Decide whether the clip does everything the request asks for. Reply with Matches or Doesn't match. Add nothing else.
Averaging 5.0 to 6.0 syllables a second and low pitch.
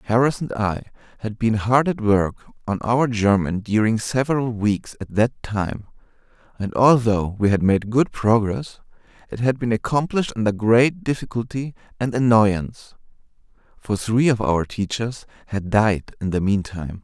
Doesn't match